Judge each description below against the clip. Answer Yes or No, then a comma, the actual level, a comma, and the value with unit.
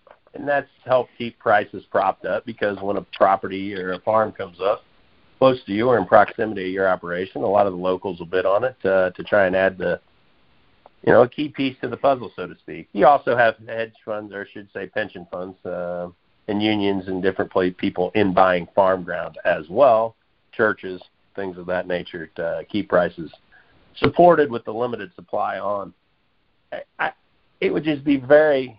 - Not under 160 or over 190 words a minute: No, average, 200 wpm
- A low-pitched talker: Yes, low, 100 Hz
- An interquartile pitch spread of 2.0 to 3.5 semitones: No, average, 4.0 semitones